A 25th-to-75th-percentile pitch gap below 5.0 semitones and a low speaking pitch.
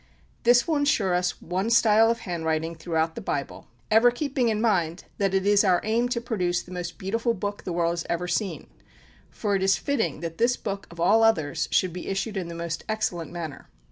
No: average, 4.6 semitones; high, 195 Hz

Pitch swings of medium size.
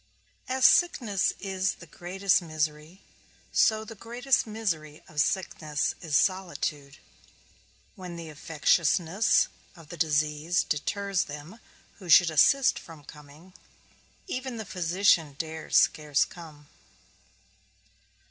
Yes: average, 4.4 semitones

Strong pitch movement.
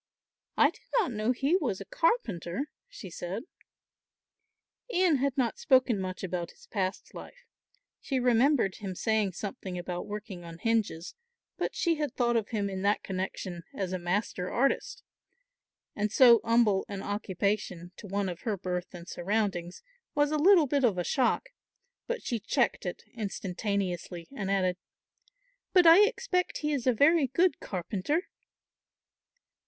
Yes: wide, 6.8 semitones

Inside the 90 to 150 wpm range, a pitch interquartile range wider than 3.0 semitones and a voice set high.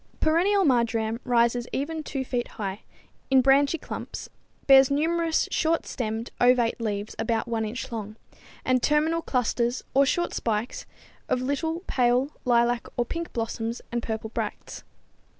Yes: average, 145 wpm; average, 3.8 semitones; high, 245 Hz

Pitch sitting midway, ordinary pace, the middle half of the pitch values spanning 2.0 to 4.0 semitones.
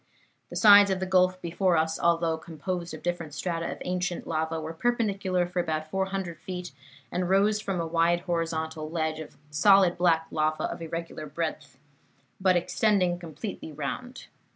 Yes: medium, 175 Hz; average, 160 wpm; average, 2.7 semitones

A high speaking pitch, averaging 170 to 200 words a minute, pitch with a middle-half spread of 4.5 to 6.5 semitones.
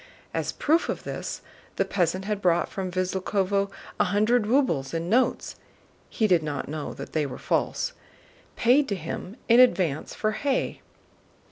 No: high, 195 Hz; average, 155 wpm; wide, 5.6 semitones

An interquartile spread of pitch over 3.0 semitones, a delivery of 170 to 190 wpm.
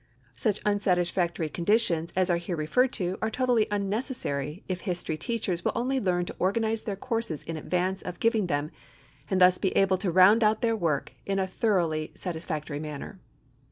Yes: average, 4.1 semitones; average, 175 wpm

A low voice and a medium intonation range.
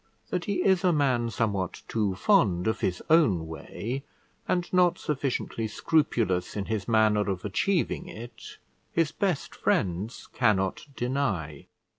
No: low, 115 Hz; wide, 7.9 semitones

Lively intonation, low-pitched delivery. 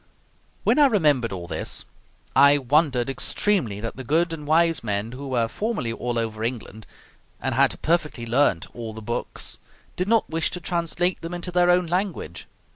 No: wide, 6.9 semitones; medium, 145 Hz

